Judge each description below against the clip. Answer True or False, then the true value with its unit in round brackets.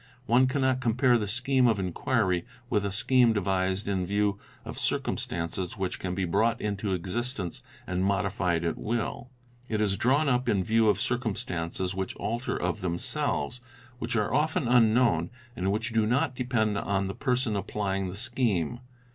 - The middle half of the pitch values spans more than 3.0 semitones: True (4.4 semitones)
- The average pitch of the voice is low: True (105 Hz)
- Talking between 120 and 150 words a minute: False (165 wpm)